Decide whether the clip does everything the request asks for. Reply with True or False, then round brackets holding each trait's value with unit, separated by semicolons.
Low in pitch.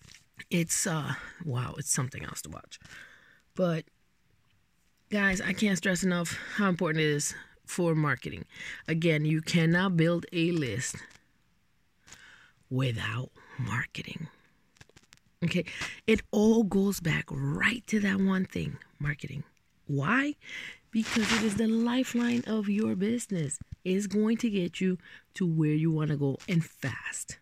False (170 Hz)